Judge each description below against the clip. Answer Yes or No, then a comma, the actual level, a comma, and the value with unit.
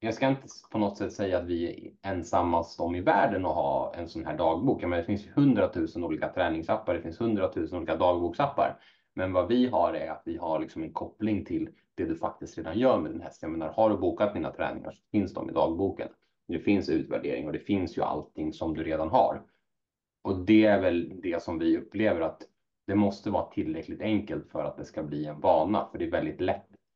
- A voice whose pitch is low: Yes, low, 100 Hz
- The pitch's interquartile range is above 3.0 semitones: Yes, average, 4.4 semitones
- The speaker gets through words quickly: Yes, fast, 220 wpm